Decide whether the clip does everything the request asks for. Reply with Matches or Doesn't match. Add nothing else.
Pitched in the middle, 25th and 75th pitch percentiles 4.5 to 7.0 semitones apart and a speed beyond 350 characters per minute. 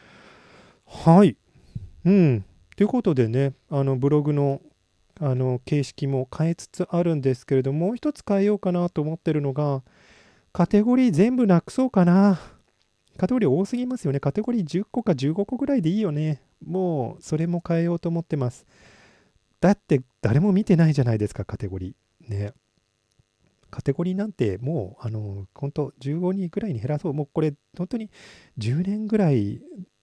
Doesn't match